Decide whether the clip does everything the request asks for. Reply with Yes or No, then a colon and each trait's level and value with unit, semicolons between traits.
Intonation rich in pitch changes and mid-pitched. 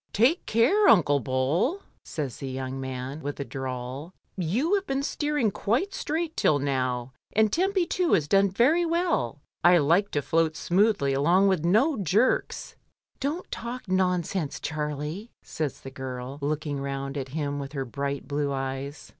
Yes: wide, 8.5 semitones; medium, 155 Hz